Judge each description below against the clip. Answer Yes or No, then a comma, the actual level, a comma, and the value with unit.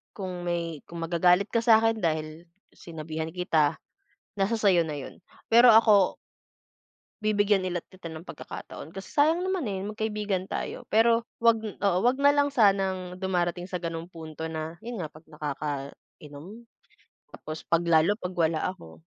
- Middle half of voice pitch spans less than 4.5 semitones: No, average, 4.8 semitones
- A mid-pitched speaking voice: Yes, medium, 180 Hz